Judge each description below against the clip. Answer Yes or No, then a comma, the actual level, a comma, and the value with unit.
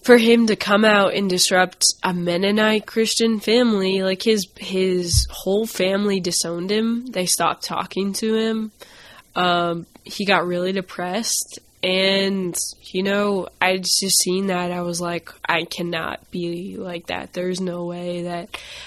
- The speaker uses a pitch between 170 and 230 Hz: Yes, medium, 185 Hz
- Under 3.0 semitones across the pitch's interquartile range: Yes, narrow, 2.6 semitones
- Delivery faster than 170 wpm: No, average, 150 wpm